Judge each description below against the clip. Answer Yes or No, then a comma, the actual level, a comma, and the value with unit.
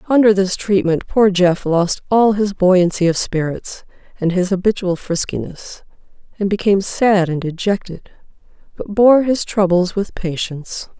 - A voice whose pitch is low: No, high, 190 Hz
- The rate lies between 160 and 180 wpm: No, average, 140 wpm